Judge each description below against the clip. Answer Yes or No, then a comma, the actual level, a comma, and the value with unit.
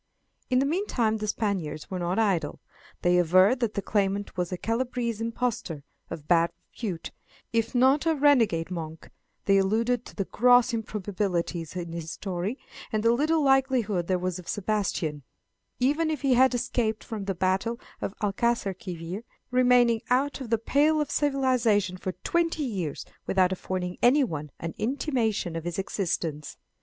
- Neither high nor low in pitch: No, high, 210 Hz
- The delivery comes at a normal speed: Yes, average, 155 wpm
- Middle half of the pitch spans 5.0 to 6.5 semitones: Yes, wide, 5.5 semitones